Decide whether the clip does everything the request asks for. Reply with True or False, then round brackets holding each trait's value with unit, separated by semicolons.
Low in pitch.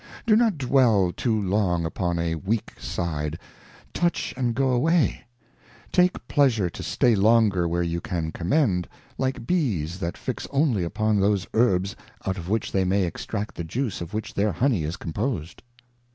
True (100 Hz)